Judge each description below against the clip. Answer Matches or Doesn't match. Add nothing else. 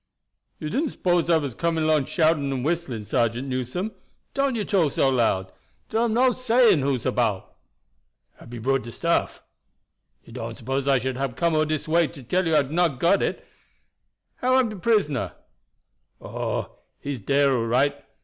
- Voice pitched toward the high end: Doesn't match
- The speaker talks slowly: Doesn't match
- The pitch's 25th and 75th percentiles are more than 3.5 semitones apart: Matches